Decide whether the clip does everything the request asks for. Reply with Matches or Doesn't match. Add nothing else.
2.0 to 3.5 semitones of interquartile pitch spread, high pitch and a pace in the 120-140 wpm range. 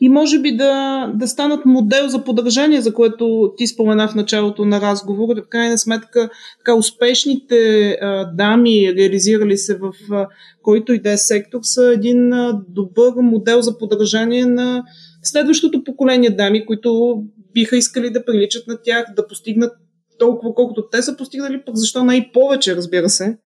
Doesn't match